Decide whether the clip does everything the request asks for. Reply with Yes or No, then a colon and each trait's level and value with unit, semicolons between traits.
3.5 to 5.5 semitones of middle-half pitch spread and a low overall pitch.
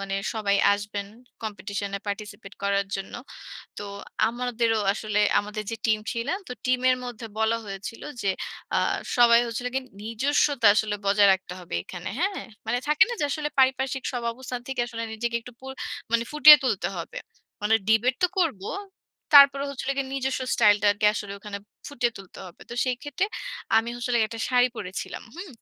No: average, 4.1 semitones; high, 230 Hz